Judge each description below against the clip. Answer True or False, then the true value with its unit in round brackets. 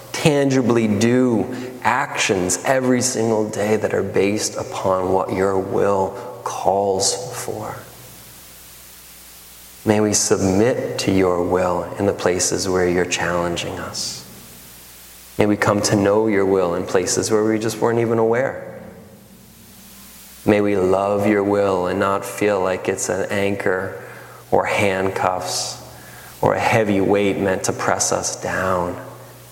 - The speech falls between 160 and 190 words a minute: False (135 wpm)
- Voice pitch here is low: True (100 Hz)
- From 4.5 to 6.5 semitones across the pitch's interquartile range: False (3.2 semitones)